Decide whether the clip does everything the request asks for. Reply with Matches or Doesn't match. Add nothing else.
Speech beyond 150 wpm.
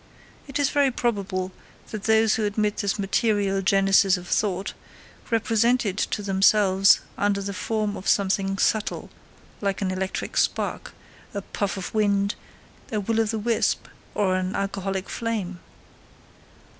Doesn't match